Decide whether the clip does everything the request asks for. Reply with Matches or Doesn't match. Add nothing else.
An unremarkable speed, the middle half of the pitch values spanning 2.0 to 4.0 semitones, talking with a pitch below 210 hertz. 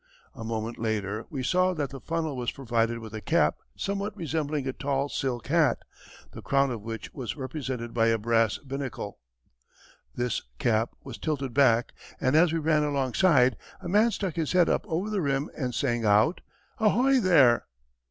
Doesn't match